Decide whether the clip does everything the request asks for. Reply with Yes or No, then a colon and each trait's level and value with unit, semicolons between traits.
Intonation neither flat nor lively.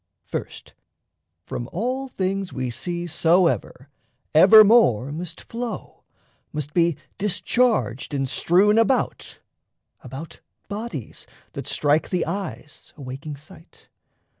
No: wide, 5.9 semitones